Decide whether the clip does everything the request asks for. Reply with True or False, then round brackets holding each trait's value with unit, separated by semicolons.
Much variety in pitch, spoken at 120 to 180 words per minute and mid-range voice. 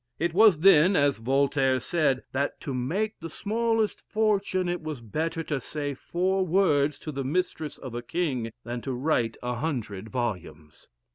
True (5.8 semitones; 165 wpm; 150 Hz)